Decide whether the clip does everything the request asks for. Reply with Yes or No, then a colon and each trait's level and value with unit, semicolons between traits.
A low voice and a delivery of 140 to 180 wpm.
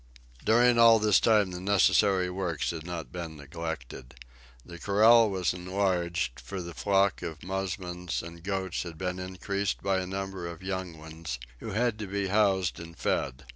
Yes: very low, 90 Hz; average, 170 wpm